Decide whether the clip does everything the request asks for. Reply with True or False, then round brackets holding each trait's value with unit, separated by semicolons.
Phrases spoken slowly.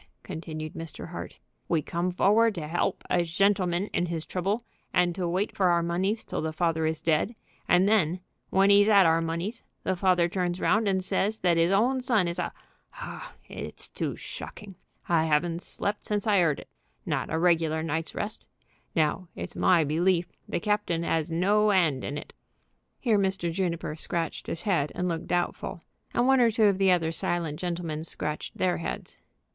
False (185 wpm)